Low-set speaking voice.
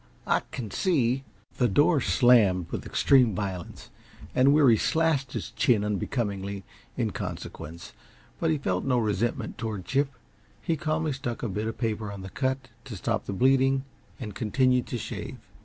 Yes: low, 120 Hz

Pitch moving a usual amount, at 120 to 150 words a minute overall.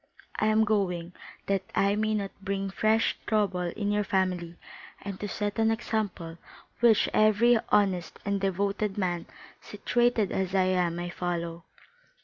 Yes: average, 3.0 semitones; average, 145 wpm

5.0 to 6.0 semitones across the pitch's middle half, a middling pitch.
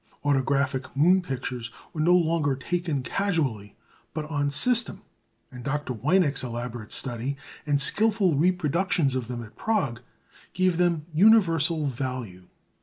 Yes: wide, 5.4 semitones; medium, 145 Hz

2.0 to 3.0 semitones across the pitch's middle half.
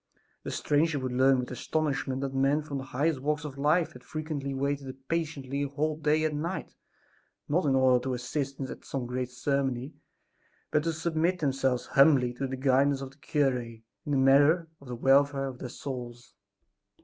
Yes: narrow, 2.4 semitones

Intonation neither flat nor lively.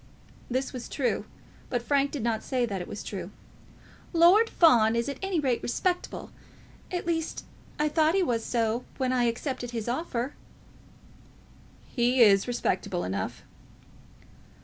Yes: average, 4.7 semitones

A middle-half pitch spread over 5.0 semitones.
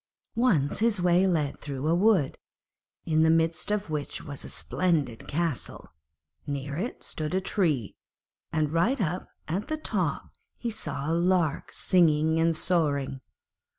No: average, 3.7 semitones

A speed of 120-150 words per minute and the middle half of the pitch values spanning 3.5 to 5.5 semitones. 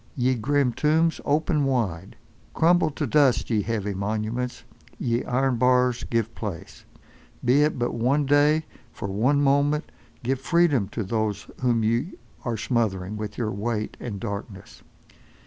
Yes: average, 145 wpm; average, 4.7 semitones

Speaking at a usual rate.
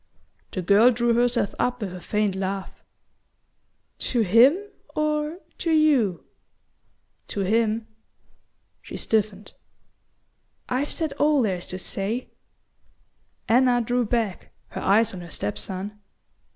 No: slow, 125 wpm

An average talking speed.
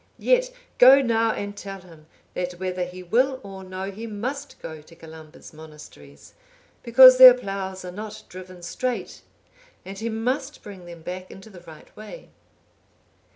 Yes: average, 155 wpm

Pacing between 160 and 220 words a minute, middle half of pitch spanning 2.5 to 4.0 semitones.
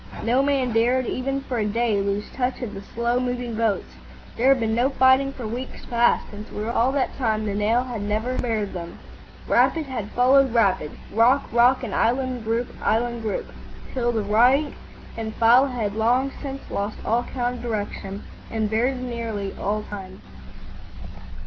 Yes: average, 175 wpm; average, 2.9 semitones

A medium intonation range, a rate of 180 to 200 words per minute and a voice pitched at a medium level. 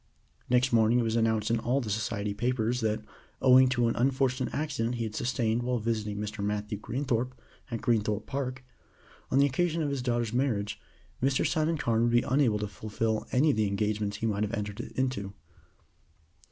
No: average, 3.2 semitones; average, 185 wpm; low, 115 Hz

